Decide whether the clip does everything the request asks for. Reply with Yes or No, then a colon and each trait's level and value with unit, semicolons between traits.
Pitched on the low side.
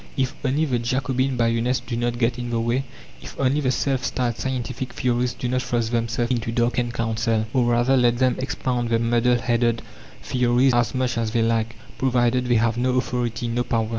Yes: low, 120 Hz